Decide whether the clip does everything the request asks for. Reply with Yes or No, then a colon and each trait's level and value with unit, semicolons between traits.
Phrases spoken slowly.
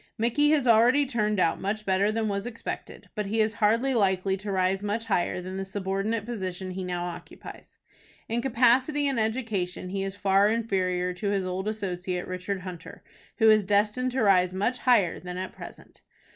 No: average, 185 wpm